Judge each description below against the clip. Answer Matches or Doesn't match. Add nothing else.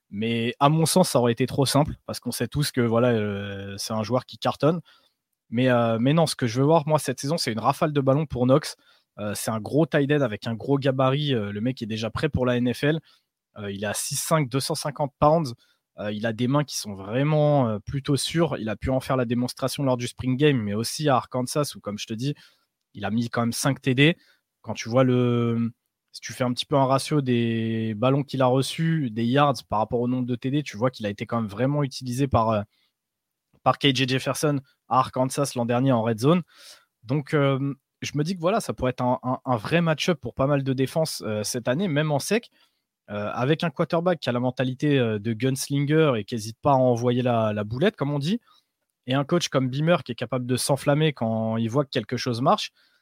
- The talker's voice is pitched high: Doesn't match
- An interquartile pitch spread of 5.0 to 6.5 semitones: Doesn't match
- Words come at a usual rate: Doesn't match